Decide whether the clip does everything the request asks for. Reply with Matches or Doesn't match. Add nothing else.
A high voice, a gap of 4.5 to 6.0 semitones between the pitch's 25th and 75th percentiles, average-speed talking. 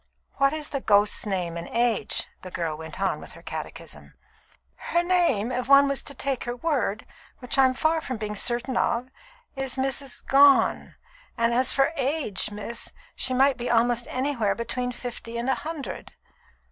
Doesn't match